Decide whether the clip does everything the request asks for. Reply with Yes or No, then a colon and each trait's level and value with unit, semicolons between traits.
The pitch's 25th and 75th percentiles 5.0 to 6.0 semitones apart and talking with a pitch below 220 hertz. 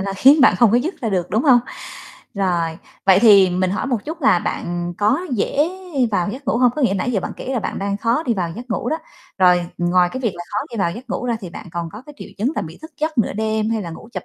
Yes: wide, 5.5 semitones; high, 210 Hz